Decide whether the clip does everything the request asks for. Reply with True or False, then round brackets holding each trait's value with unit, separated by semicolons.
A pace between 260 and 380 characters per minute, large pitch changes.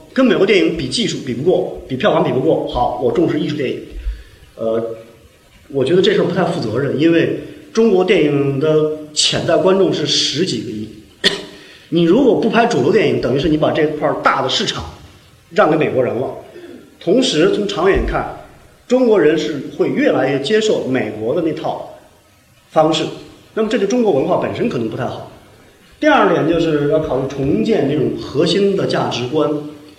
True (270 characters per minute; 6.4 semitones)